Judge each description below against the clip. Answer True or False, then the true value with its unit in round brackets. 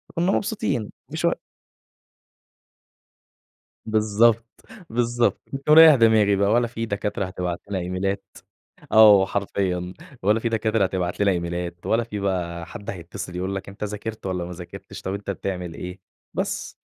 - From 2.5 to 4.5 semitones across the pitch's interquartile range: True (3.6 semitones)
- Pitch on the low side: True (100 Hz)